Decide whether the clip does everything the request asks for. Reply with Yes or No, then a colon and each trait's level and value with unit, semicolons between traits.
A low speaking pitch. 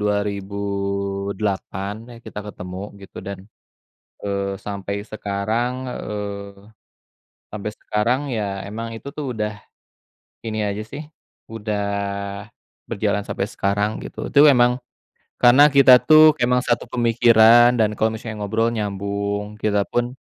Yes: low, 105 Hz